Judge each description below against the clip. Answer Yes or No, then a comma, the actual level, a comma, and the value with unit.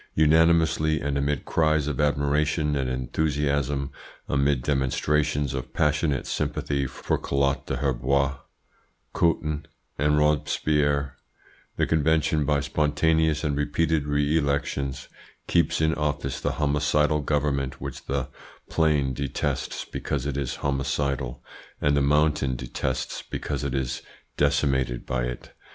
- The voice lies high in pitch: No, very low, 70 Hz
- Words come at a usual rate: No, slow, 120 wpm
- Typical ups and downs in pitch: No, narrow, 1.6 semitones